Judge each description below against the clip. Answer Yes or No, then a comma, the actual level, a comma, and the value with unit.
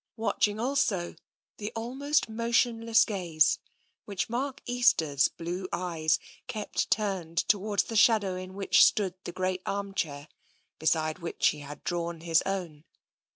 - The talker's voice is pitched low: No, high, 190 Hz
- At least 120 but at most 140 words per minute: Yes, slow, 135 wpm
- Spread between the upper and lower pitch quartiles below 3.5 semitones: No, average, 4.9 semitones